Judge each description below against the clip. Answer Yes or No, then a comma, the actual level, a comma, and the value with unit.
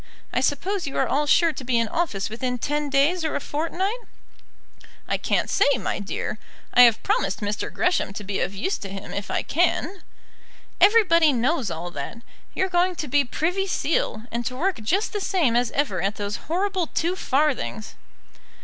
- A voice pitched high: Yes, very high, 285 Hz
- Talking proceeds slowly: No, average, 185 wpm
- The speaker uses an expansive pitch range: Yes, wide, 7.9 semitones